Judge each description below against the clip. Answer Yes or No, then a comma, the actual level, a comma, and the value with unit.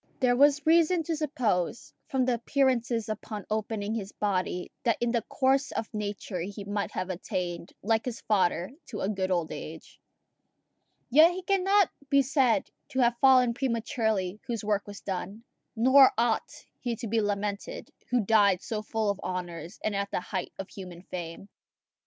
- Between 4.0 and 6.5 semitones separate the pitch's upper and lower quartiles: Yes, average, 4.6 semitones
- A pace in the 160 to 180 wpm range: Yes, average, 170 wpm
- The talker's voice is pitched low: No, high, 220 Hz